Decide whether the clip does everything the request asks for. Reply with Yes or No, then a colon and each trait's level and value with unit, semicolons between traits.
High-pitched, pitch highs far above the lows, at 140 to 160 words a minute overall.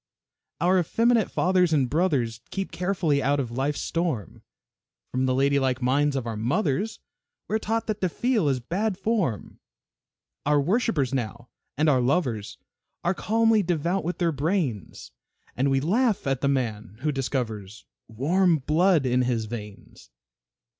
No: medium, 145 Hz; wide, 6.5 semitones; average, 150 wpm